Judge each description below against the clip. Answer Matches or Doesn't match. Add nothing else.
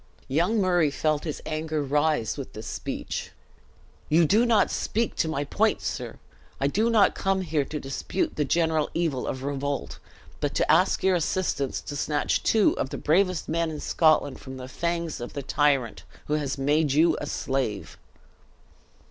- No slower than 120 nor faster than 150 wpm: Doesn't match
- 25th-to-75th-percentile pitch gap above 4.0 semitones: Doesn't match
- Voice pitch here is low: Doesn't match